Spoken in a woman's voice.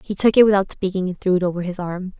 Yes: female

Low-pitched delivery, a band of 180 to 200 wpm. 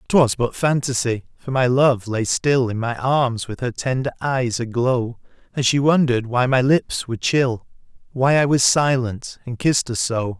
Yes: low, 125 Hz; average, 185 wpm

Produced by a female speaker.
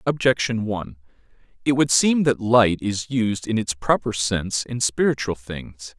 No: male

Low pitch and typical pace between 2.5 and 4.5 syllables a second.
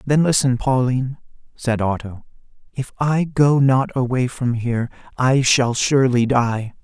Yes: low, 125 Hz; 4.4 syllables/s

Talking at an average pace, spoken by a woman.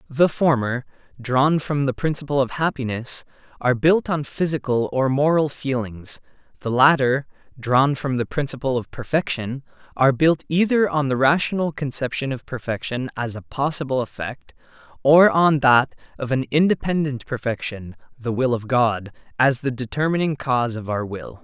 No: average, 150 wpm; male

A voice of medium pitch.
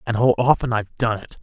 No: low, 115 Hz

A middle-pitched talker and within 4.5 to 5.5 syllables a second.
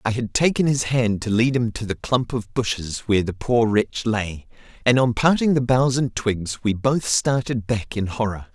No: low, 115 Hz; 4.6 syllables/s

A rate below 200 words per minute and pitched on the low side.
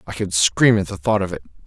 No: fast, 290 wpm; very low, 95 Hz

